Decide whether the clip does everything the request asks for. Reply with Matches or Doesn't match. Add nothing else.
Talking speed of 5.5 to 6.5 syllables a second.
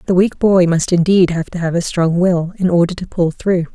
Doesn't match